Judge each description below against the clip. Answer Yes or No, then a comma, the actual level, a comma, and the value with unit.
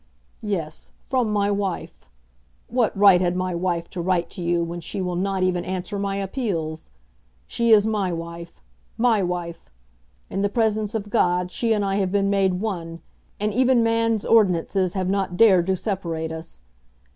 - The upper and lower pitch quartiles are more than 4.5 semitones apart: No, average, 3.0 semitones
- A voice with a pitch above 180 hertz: Yes, high, 190 Hz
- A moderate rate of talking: Yes, average, 170 wpm